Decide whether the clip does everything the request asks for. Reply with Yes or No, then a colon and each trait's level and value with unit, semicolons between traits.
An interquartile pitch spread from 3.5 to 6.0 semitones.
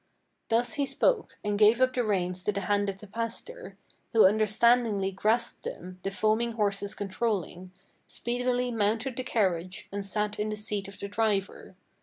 No: average, 2.9 semitones